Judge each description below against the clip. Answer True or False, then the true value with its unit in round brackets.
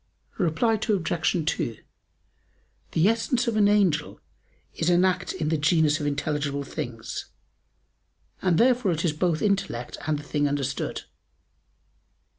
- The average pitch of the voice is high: False (165 Hz)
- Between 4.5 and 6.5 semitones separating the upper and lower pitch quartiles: True (4.8 semitones)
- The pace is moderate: False (130 wpm)